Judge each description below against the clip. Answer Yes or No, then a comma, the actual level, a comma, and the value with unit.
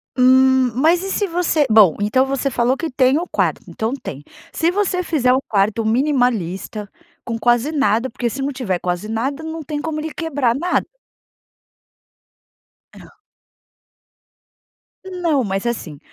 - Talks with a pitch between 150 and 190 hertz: No, very high, 260 Hz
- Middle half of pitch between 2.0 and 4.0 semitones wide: No, wide, 5.6 semitones